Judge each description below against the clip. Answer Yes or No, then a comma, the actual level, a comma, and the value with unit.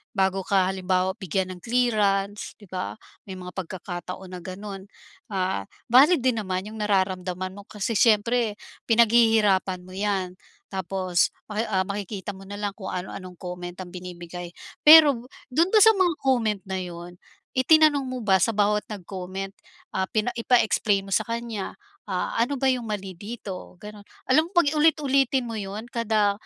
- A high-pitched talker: Yes, high, 200 Hz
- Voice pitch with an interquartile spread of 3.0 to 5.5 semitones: Yes, average, 3.8 semitones